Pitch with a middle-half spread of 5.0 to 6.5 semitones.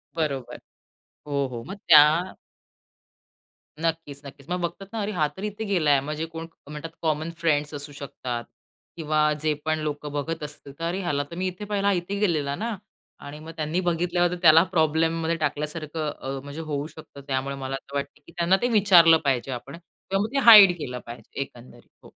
No: average, 3.4 semitones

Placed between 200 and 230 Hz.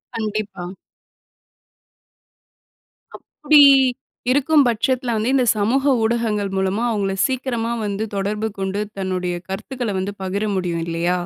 Yes: high, 210 Hz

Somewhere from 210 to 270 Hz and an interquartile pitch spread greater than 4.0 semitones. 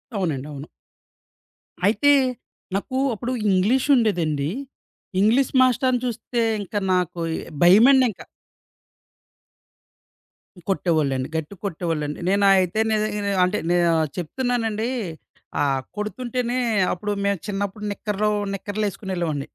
No: high, 200 Hz; average, 4.6 semitones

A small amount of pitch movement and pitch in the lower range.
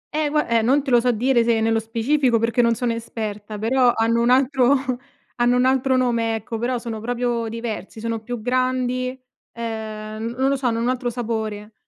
No: narrow, 2.0 semitones; high, 235 Hz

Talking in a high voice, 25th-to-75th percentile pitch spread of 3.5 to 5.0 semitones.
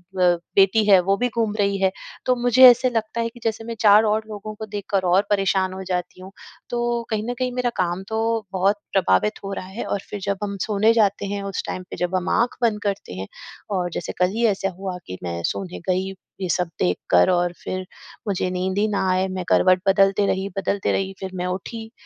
No: high, 195 Hz; average, 2.8 semitones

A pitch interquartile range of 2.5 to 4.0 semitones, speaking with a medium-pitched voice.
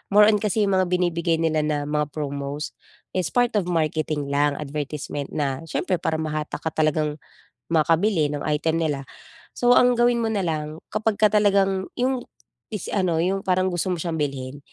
No: average, 4.5 semitones; medium, 165 Hz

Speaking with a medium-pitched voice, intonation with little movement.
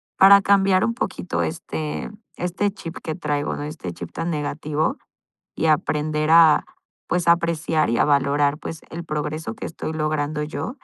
Yes: medium, 155 Hz; narrow, 2.3 semitones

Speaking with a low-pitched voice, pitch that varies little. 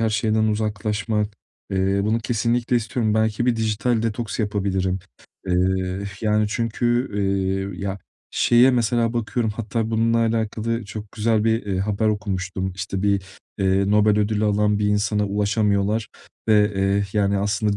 Yes: low, 105 Hz; narrow, 2.1 semitones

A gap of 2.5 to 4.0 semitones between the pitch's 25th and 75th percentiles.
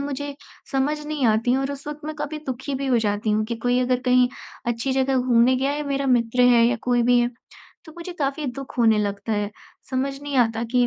Yes: average, 2.9 semitones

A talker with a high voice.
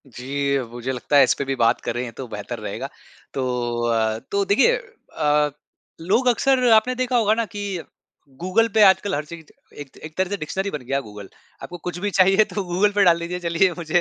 No: medium, 175 Hz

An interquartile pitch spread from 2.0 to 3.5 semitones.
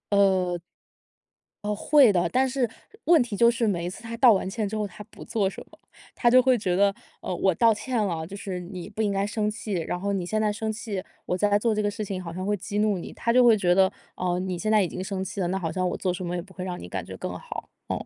Yes: average, 3.1 semitones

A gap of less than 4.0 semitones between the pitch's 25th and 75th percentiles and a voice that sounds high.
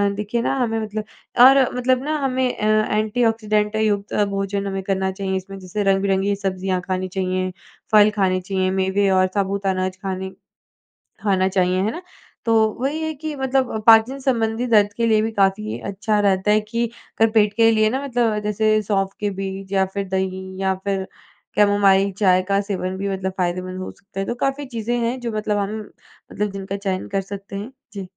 Yes: narrow, 2.5 semitones; high, 200 Hz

